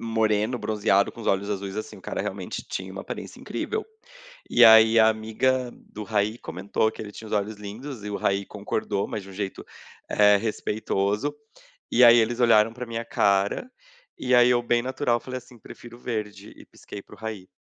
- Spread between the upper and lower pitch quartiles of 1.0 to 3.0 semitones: Yes, narrow, 2.6 semitones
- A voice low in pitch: Yes, low, 110 Hz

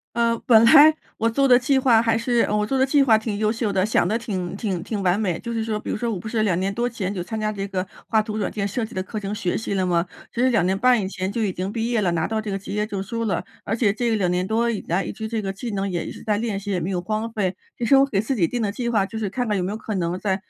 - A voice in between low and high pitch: No, high, 215 Hz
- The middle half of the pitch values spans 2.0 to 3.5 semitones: Yes, average, 3.1 semitones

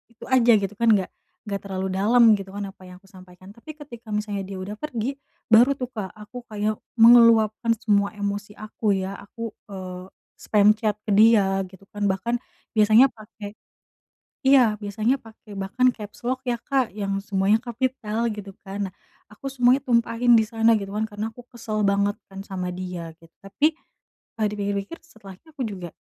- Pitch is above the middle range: Yes, high, 210 Hz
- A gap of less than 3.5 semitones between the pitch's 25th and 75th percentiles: Yes, average, 3.0 semitones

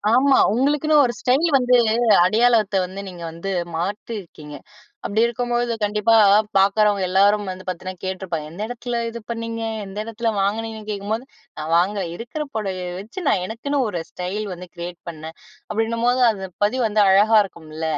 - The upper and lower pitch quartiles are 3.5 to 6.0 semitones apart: Yes, average, 3.9 semitones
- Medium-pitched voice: No, high, 210 Hz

